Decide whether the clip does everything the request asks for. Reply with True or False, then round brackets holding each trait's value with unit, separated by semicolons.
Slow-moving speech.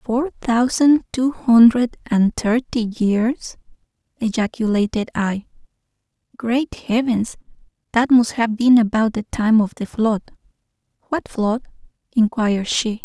True (115 wpm)